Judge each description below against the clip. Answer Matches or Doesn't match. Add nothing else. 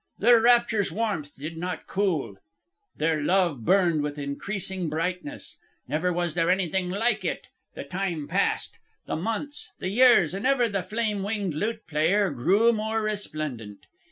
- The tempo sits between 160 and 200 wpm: Doesn't match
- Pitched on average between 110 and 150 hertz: Doesn't match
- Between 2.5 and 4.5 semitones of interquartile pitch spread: Doesn't match